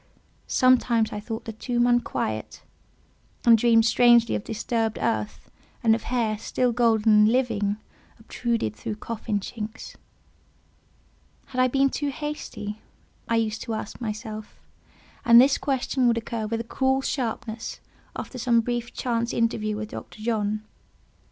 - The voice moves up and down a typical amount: No, narrow, 2.0 semitones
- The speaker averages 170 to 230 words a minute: No, average, 140 wpm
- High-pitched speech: Yes, high, 230 Hz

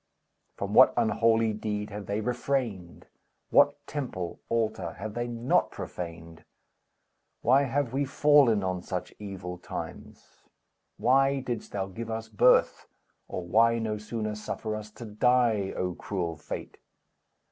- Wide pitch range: No, average, 3.6 semitones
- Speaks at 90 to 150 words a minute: Yes, slow, 135 wpm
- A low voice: Yes, low, 110 Hz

